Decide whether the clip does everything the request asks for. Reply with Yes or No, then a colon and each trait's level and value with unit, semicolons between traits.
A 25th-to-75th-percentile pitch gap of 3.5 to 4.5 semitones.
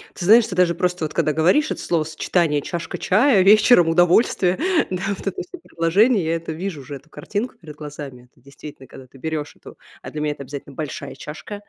Yes: average, 4.1 semitones